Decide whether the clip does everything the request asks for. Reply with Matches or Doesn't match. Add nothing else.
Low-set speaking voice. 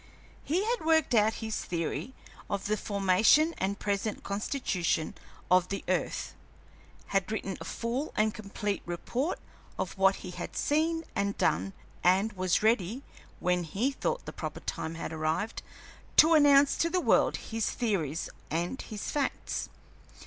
Doesn't match